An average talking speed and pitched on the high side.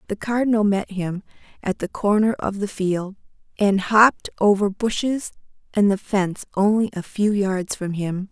Yes: average, 165 wpm; high, 200 Hz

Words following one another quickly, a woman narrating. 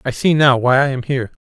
No: fast, 295 wpm; male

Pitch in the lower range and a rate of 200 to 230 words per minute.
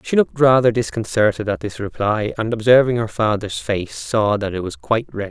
Yes: low, 110 Hz; fast, 205 wpm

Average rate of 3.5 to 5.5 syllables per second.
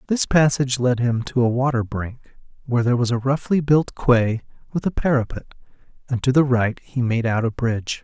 No: 5.8 syllables/s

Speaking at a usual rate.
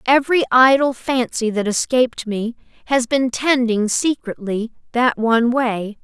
No: slow, 130 wpm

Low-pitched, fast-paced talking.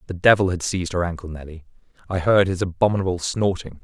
No: very low, 90 Hz; average, 190 wpm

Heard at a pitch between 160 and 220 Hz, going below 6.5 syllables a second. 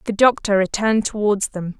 Yes: high, 205 Hz; 5.5 syllables/s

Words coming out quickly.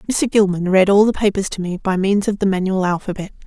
Yes: fast, 240 wpm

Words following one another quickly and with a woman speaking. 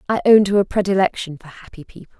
Yes: fast, 220 wpm; female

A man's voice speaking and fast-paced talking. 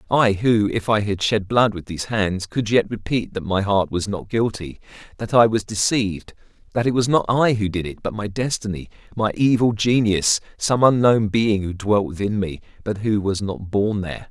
Yes: male; fast, 210 wpm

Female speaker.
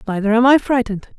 Yes: female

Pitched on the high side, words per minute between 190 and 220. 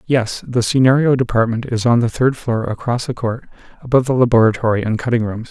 No: low, 120 Hz; average, 195 wpm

